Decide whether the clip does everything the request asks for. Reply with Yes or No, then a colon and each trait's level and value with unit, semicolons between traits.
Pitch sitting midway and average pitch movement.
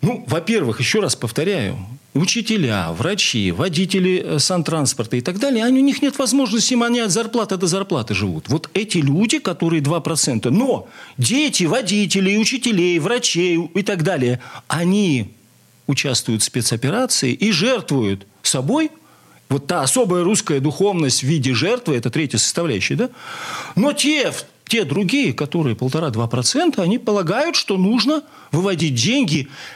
No: medium, 175 Hz; wide, 8.4 semitones